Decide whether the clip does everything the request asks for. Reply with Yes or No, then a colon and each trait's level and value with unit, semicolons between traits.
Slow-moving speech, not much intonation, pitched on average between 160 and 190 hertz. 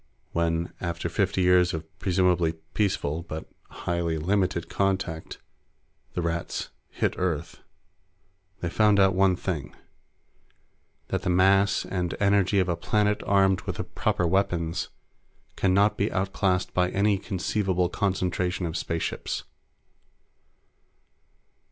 No: slow, 120 wpm; narrow, 2.3 semitones; very low, 90 Hz